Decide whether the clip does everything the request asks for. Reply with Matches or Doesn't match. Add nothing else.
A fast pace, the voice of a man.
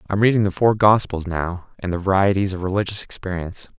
Doesn't match